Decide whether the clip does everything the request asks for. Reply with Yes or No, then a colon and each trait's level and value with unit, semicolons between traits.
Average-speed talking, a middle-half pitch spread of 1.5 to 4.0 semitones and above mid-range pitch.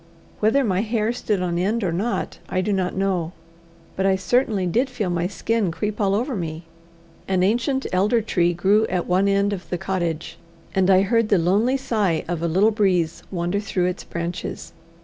Yes: average, 190 wpm; average, 3.3 semitones; high, 195 Hz